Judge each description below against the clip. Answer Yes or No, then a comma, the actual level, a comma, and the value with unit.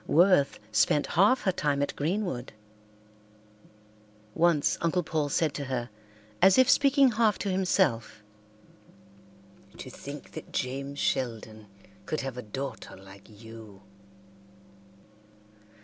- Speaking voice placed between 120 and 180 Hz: Yes, medium, 140 Hz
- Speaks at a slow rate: Yes, slow, 115 wpm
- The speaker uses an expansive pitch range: Yes, wide, 8.1 semitones